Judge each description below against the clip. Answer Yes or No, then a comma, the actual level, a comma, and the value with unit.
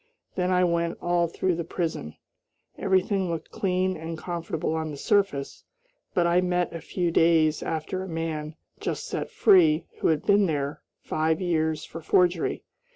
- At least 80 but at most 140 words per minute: No, average, 160 wpm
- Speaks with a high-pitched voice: No, medium, 170 Hz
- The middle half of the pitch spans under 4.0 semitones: Yes, narrow, 2.4 semitones